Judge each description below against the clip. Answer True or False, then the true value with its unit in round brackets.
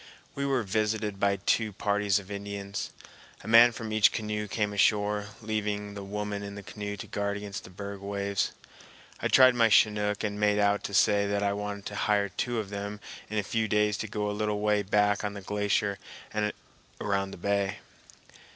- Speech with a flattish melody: True (0.8 semitones)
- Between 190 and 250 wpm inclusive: True (195 wpm)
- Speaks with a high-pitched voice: False (105 Hz)